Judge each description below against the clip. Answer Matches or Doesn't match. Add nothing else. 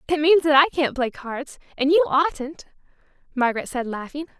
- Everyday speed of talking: Matches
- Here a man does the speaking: Doesn't match